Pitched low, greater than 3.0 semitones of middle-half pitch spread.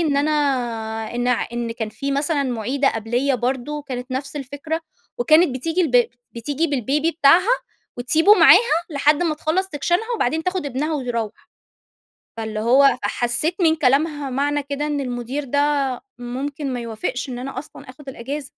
No: very high, 280 Hz; average, 3.6 semitones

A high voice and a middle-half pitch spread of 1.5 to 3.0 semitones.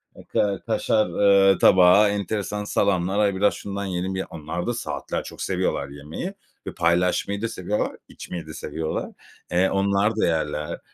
No: very low, 95 Hz; average, 2.7 semitones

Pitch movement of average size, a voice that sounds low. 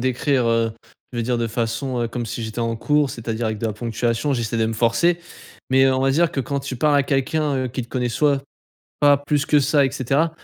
Yes: average, 3.5 semitones; low, 130 Hz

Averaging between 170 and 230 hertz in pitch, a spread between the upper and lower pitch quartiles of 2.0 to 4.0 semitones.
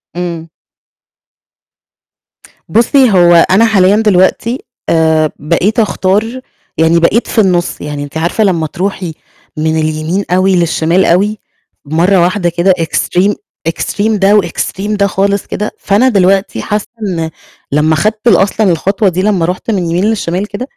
Yes: medium, 185 Hz; average, 3.7 semitones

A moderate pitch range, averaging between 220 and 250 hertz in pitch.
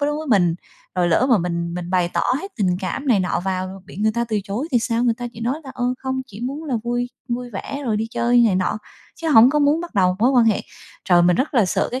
No: wide, 5.7 semitones; high, 230 Hz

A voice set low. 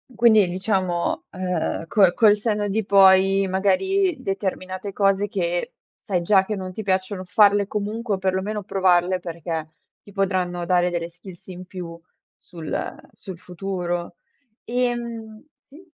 No: high, 190 Hz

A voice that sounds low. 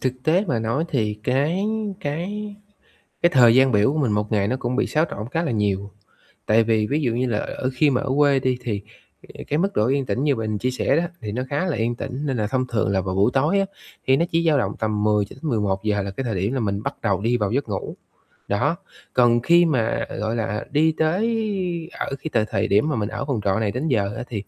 Yes: low, 120 Hz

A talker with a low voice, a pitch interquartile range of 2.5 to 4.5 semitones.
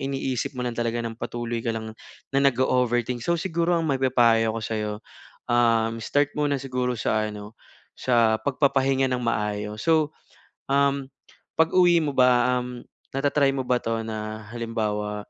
Yes: low, 125 Hz; average, 3.4 semitones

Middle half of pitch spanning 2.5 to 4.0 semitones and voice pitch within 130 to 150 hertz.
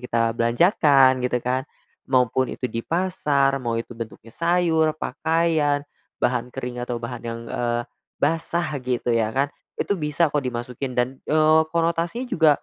No: average, 4.7 semitones; low, 135 Hz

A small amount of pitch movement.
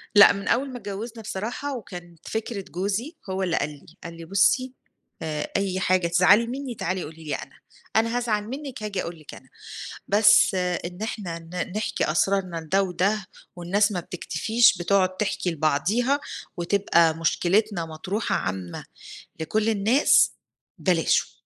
No: average, 4.1 semitones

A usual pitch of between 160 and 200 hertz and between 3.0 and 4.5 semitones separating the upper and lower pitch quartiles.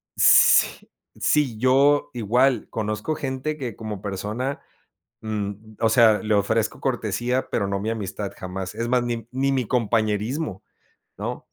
No: low, 115 Hz; average, 3.6 semitones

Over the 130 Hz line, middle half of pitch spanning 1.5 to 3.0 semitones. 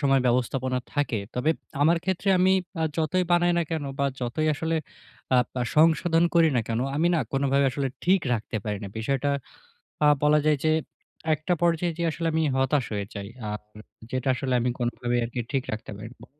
No: medium, 140 Hz; average, 4.9 semitones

